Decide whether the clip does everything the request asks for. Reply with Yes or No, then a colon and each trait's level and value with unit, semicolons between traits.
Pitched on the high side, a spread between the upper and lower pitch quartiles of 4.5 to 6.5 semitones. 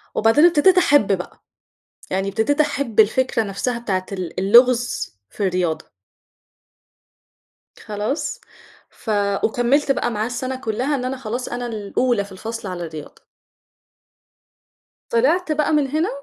Yes: high, 235 Hz; average, 5.2 semitones